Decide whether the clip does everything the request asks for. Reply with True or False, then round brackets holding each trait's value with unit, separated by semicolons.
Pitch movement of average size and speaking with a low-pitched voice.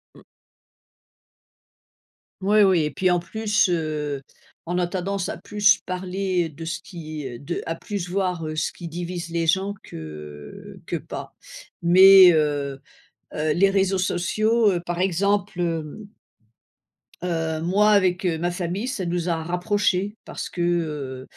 False (3.1 semitones; 175 Hz)